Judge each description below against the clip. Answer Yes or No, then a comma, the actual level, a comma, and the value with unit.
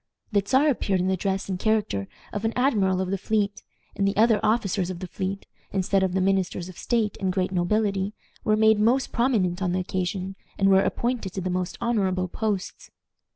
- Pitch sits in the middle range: No, high, 195 Hz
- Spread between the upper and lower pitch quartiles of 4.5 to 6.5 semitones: No, average, 2.7 semitones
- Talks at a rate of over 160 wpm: Yes, average, 200 wpm